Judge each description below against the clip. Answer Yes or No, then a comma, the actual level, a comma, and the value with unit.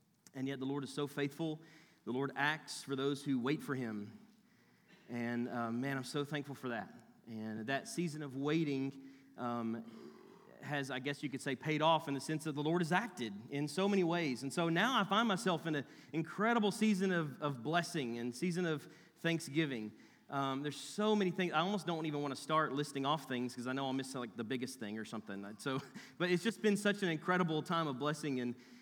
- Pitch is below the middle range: No, medium, 145 Hz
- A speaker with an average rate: No, fast, 220 wpm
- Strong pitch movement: No, average, 4.0 semitones